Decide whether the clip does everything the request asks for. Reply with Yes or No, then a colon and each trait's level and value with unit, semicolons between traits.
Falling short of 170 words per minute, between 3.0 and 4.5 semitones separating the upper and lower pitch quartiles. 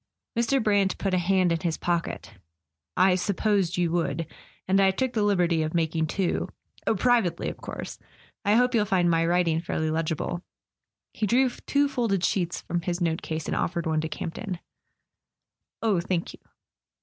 No: average, 175 wpm; average, 3.6 semitones